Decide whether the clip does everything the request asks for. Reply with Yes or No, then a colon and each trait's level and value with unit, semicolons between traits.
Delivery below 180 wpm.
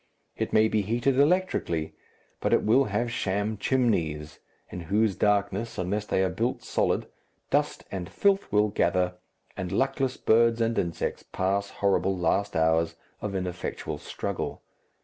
Yes: average, 145 wpm